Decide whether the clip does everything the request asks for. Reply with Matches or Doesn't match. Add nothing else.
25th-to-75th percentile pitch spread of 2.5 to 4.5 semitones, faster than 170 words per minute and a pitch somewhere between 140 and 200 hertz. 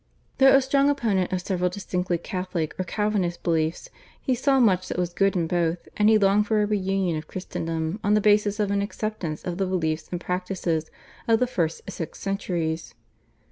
Matches